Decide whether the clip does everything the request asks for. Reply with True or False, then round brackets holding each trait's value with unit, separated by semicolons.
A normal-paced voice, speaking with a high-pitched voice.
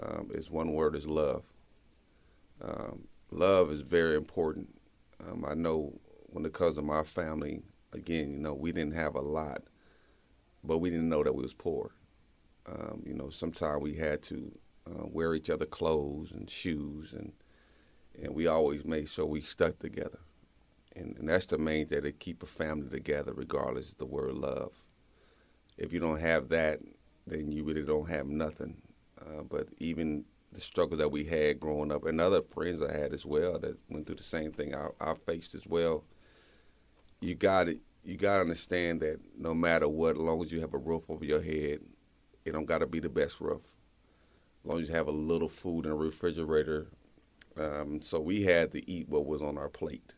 False (195 wpm; 75 Hz)